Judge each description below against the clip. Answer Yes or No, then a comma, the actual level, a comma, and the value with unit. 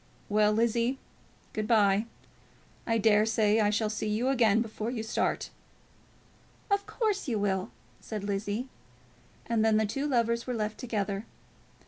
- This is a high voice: Yes, high, 220 Hz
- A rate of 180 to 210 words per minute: No, average, 145 wpm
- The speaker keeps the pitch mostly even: Yes, narrow, 1.9 semitones